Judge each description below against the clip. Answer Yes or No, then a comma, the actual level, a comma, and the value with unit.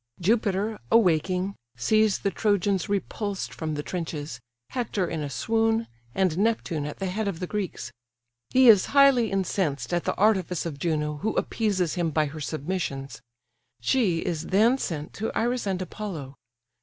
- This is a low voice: No, medium, 185 Hz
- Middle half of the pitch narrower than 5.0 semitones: No, wide, 5.4 semitones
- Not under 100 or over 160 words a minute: Yes, average, 155 wpm